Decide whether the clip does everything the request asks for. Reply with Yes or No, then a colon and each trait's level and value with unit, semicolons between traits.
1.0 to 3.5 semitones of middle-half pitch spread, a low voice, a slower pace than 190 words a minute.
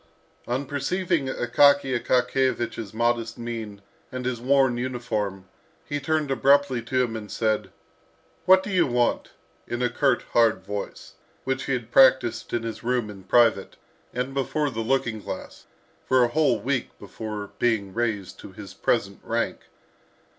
Yes: average, 3.2 semitones; low, 120 Hz; average, 150 wpm